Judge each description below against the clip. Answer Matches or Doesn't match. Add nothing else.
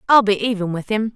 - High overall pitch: Matches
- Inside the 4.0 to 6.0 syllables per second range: Doesn't match